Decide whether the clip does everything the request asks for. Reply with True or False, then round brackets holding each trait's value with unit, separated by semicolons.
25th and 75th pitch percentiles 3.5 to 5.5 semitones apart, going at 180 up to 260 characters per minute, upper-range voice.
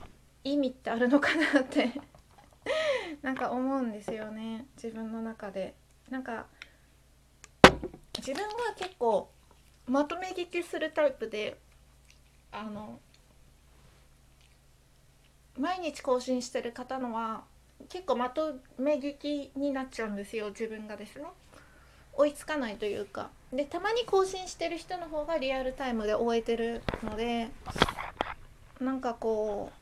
True (5.1 semitones; 245 characters per minute; 260 Hz)